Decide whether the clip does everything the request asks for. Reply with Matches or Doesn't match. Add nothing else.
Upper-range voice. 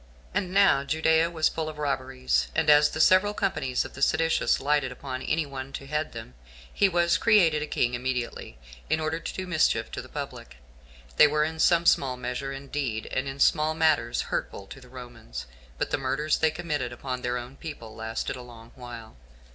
Doesn't match